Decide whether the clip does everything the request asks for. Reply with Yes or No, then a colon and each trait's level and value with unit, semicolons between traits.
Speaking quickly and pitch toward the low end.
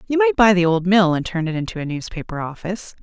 No: fast, 260 wpm; high, 190 Hz